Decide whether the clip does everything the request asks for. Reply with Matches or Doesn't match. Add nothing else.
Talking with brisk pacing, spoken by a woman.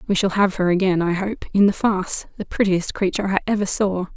Matches